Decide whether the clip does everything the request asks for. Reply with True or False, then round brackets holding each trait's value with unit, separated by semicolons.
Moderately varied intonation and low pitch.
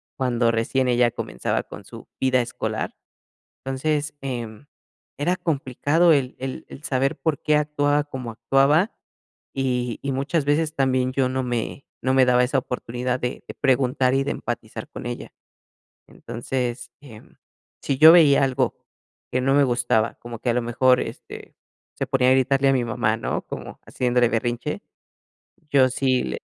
False (2.2 semitones; 130 Hz)